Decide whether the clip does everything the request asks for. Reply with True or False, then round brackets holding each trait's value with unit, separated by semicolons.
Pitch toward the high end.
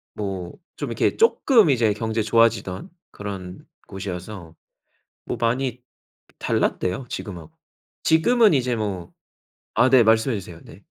False (110 Hz)